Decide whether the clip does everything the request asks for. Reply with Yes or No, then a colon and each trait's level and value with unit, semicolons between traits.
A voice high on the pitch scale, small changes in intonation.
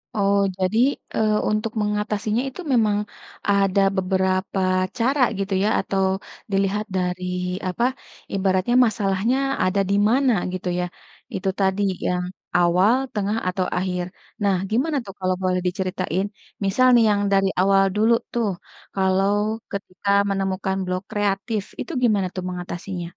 Yes: high, 195 Hz; narrow, 2.2 semitones